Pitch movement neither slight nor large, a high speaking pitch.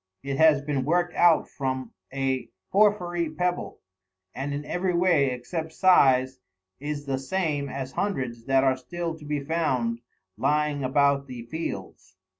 No: average, 4.0 semitones; medium, 145 Hz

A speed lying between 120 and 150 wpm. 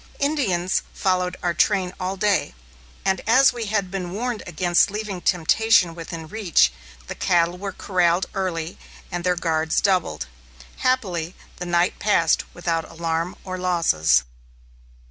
Yes: average, 140 wpm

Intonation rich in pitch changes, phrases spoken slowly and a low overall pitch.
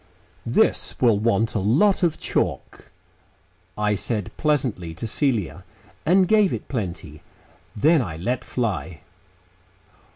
Yes: wide, 7.2 semitones; slow, 120 wpm; low, 115 Hz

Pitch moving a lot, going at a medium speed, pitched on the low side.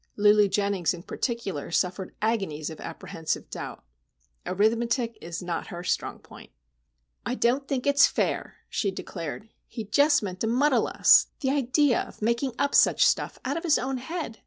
No: wide, 6.1 semitones; average, 165 wpm; high, 225 Hz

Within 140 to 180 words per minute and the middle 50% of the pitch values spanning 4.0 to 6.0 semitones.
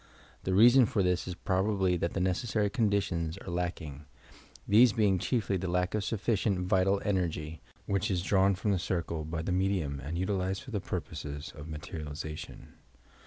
No: average, 165 wpm; average, 3.1 semitones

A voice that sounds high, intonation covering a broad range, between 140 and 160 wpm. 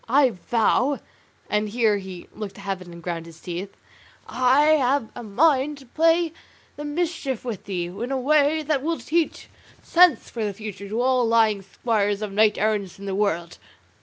No: high, 225 Hz; wide, 6.0 semitones; average, 180 wpm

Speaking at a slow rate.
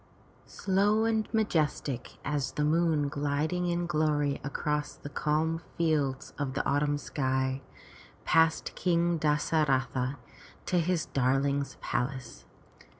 Yes: slow, 120 wpm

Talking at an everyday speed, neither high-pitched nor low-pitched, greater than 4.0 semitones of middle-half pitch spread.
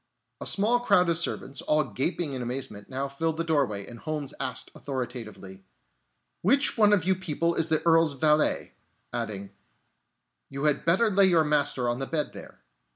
Yes: average, 170 wpm; medium, 150 Hz; average, 4.7 semitones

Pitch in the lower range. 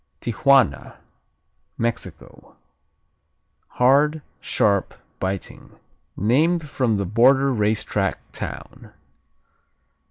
Yes: low, 120 Hz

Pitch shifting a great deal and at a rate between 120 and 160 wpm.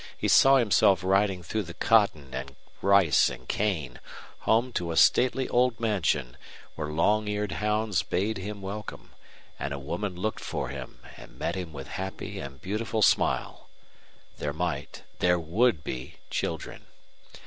Yes: wide, 5.7 semitones; average, 150 wpm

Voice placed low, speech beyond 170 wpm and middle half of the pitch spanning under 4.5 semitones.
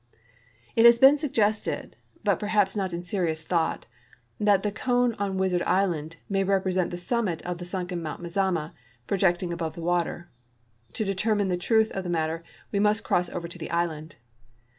No: medium, 185 Hz; average, 180 wpm; average, 3.2 semitones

